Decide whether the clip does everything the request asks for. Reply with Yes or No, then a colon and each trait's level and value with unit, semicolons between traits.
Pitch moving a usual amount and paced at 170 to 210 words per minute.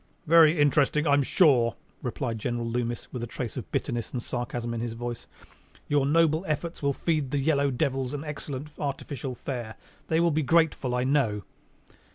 Yes: average, 3.7 semitones; average, 190 wpm